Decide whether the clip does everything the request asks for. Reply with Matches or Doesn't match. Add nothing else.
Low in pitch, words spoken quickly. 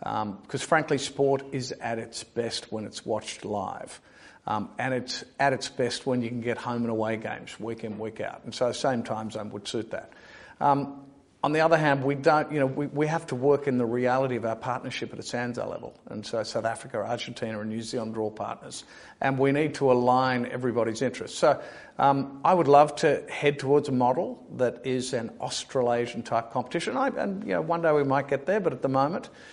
Matches